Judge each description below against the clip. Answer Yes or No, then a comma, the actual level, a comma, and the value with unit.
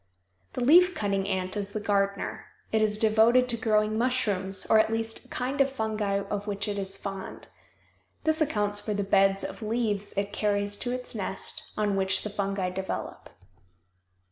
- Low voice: No, high, 210 Hz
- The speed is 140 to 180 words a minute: Yes, average, 175 wpm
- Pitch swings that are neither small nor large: No, narrow, 2.1 semitones